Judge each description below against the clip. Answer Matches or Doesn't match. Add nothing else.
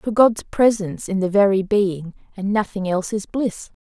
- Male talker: Doesn't match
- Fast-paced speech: Doesn't match